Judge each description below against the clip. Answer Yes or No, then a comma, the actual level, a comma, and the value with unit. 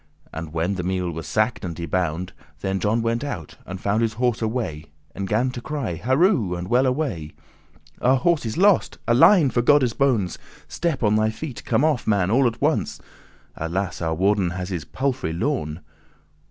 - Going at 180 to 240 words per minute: Yes, average, 185 wpm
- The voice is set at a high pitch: No, low, 110 Hz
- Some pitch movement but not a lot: No, wide, 6.2 semitones